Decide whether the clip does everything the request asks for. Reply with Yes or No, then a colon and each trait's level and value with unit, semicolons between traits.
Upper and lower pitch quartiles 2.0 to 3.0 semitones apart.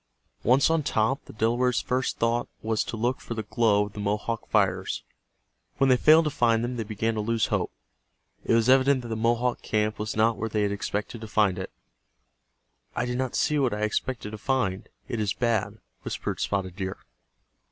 Yes: average, 2.7 semitones